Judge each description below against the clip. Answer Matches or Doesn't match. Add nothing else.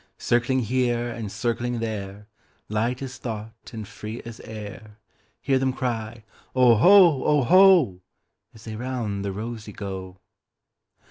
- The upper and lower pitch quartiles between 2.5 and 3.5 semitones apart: Matches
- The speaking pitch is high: Doesn't match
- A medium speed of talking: Doesn't match